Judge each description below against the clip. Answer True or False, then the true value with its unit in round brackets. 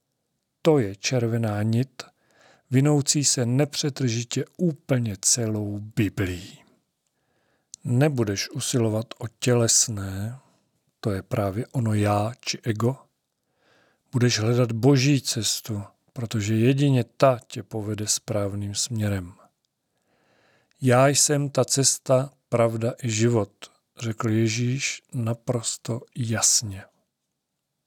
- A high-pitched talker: False (120 Hz)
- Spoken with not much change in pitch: False (3.5 semitones)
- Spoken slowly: True (95 wpm)